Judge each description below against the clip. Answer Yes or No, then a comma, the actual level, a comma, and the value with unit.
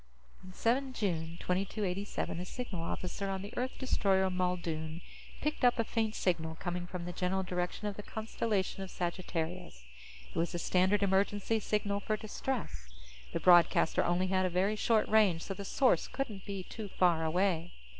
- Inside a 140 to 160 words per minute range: No, average, 170 wpm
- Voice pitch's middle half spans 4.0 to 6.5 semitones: No, average, 2.9 semitones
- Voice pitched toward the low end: No, high, 190 Hz